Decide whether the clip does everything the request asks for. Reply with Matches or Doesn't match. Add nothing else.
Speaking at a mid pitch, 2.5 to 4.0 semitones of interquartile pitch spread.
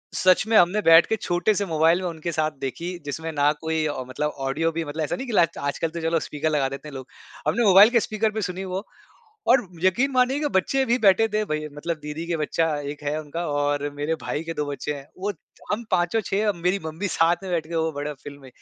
Doesn't match